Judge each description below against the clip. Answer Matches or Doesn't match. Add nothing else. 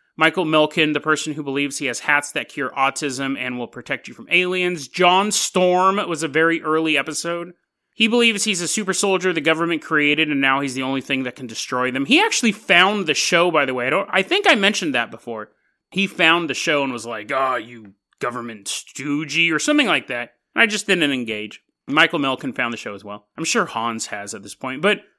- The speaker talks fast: Matches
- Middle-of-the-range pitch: Matches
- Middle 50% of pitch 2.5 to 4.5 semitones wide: Doesn't match